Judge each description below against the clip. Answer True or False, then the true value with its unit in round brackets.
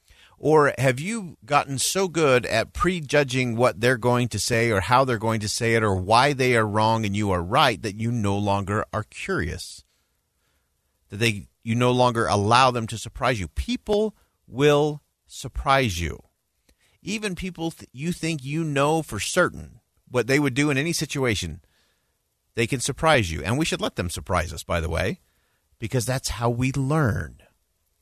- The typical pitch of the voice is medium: False (120 Hz)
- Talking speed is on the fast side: False (180 wpm)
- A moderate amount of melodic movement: False (6.5 semitones)